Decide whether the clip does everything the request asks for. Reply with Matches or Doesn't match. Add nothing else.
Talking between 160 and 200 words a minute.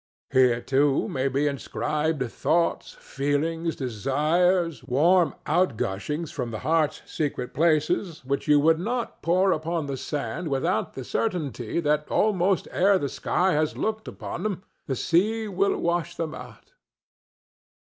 Doesn't match